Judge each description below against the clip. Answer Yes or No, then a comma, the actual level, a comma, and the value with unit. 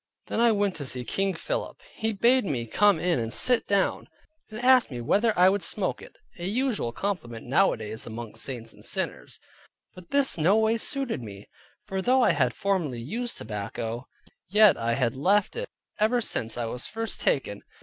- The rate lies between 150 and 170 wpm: No, average, 185 wpm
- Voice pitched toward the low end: No, high, 190 Hz